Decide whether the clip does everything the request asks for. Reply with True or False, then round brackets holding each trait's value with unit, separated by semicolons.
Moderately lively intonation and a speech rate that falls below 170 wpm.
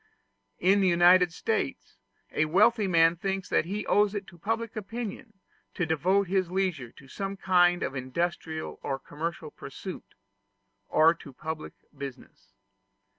True (3.8 semitones; 140 wpm)